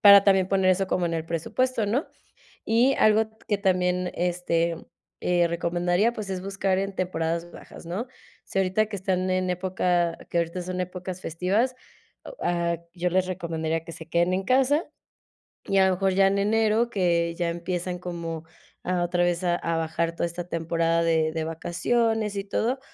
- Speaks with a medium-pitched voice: Yes, medium, 180 Hz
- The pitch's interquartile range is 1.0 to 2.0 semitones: No, narrow, 2.6 semitones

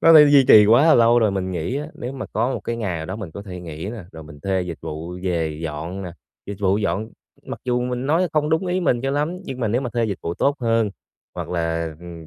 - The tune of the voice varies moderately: No, wide, 6.3 semitones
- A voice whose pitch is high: No, low, 105 Hz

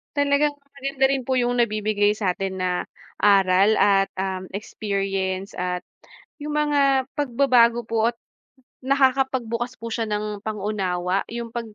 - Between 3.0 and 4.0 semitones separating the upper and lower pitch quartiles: No, average, 4.9 semitones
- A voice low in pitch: No, high, 225 Hz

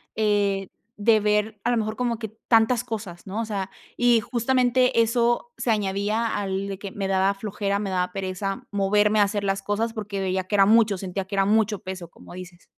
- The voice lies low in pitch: No, high, 205 Hz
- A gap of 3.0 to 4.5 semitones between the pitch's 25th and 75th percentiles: No, narrow, 2.4 semitones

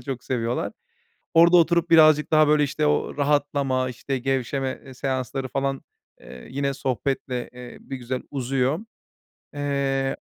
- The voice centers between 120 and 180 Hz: Yes, low, 135 Hz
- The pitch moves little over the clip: Yes, narrow, 2.1 semitones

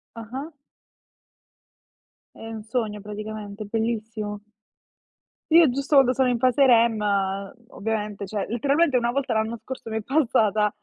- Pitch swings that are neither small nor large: Yes, average, 3.2 semitones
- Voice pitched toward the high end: Yes, high, 225 Hz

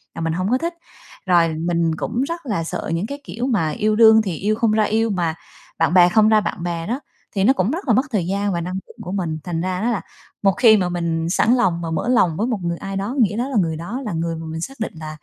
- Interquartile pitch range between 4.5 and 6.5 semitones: Yes, average, 4.9 semitones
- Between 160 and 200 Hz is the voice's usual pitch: Yes, high, 195 Hz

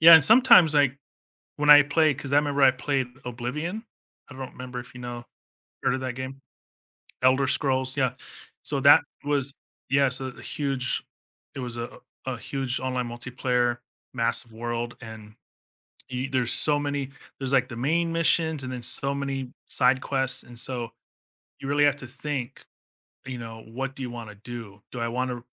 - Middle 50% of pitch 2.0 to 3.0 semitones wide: Yes, narrow, 2.5 semitones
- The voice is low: Yes, low, 130 Hz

